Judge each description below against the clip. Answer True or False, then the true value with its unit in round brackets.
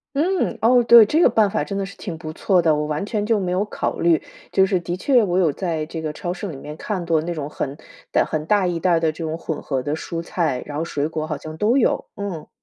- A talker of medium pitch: True (170 Hz)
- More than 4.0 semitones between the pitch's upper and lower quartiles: True (4.4 semitones)